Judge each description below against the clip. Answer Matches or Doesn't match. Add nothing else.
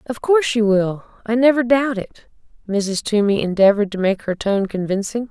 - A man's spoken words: Doesn't match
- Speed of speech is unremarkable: Matches